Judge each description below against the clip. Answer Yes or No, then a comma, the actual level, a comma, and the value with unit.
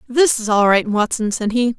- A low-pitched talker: No, high, 230 Hz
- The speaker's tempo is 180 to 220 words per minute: No, fast, 235 wpm